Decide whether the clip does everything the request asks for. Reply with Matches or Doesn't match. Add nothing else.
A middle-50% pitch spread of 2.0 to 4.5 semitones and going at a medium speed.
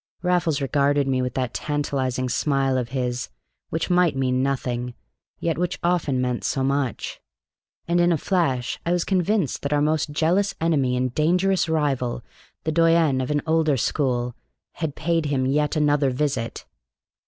Matches